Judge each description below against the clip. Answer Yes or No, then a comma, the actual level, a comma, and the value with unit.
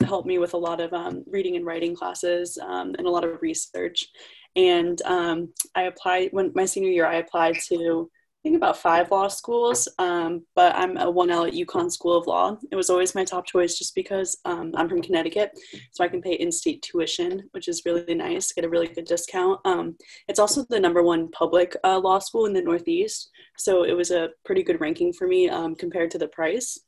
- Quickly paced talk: Yes, fast, 220 wpm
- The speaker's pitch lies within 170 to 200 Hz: Yes, medium, 185 Hz